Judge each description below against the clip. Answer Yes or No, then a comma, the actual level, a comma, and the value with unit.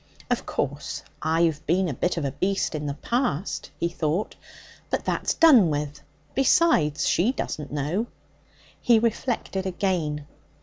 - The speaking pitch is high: No, medium, 170 Hz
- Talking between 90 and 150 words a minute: Yes, average, 140 wpm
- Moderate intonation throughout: No, wide, 6.1 semitones